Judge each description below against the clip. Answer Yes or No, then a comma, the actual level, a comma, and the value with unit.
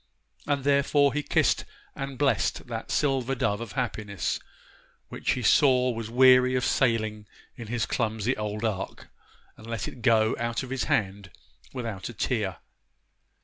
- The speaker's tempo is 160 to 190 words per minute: No, average, 150 wpm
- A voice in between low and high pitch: No, low, 115 Hz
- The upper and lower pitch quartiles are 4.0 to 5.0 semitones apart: No, average, 3.3 semitones